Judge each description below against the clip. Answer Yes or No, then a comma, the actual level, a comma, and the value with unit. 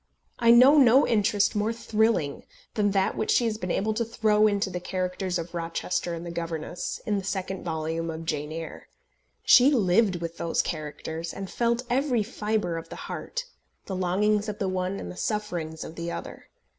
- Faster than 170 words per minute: Yes, average, 190 wpm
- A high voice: Yes, high, 195 Hz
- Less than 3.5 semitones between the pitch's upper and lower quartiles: No, average, 4.4 semitones